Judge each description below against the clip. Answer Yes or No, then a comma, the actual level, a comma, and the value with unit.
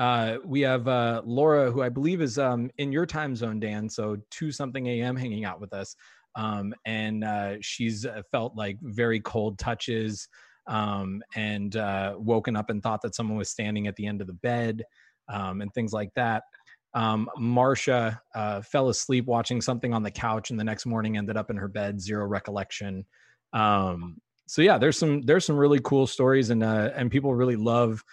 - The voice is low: Yes, low, 110 Hz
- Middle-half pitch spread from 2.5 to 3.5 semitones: Yes, average, 2.9 semitones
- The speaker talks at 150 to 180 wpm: No, average, 195 wpm